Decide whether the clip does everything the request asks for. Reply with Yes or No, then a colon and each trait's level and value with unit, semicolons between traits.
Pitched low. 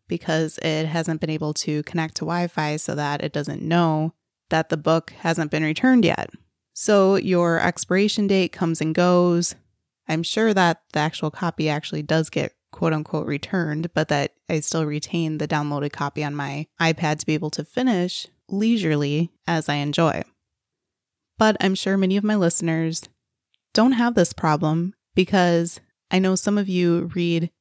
No: medium, 165 Hz